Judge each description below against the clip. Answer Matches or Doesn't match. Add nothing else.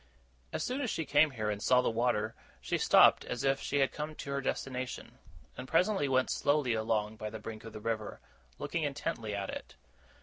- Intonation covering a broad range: Doesn't match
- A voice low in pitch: Matches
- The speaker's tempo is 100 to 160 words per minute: Doesn't match